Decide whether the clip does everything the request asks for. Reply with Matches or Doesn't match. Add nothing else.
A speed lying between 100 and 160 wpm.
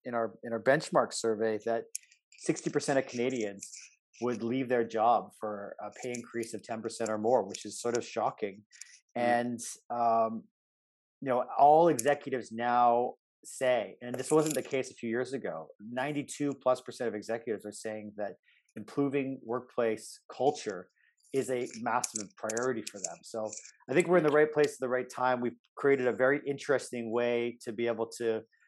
Doesn't match